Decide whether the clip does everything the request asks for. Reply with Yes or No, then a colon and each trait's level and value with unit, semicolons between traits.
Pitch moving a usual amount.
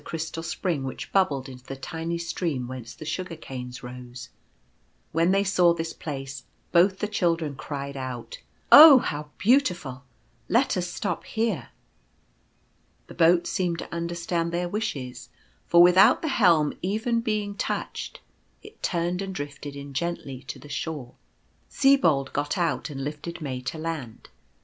Yes: average, 4.9 semitones